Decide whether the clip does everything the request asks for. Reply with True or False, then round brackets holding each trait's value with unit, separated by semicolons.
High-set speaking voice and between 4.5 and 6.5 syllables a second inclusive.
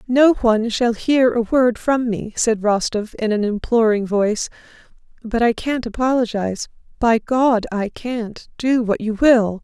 False (230 Hz; 4.3 syllables/s)